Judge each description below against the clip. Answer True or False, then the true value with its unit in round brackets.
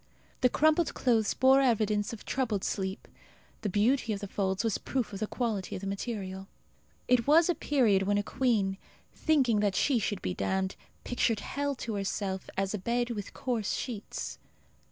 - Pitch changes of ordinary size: True (4.1 semitones)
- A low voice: False (215 Hz)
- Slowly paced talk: False (175 wpm)